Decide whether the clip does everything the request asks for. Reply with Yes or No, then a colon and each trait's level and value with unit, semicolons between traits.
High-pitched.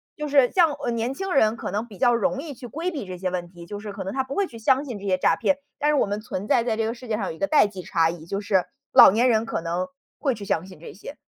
Yes: high, 225 Hz